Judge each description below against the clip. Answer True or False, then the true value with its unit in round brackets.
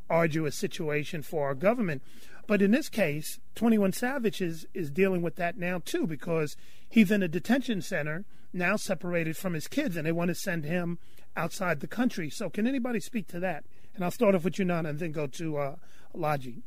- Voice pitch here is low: False (180 Hz)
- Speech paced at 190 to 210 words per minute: True (205 wpm)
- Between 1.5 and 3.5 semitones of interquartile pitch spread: False (4.0 semitones)